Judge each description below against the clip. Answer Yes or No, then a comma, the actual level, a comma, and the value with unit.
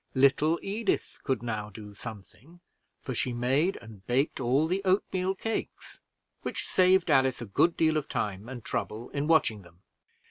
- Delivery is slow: No, average, 165 wpm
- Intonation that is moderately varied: No, wide, 6.9 semitones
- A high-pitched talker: No, low, 130 Hz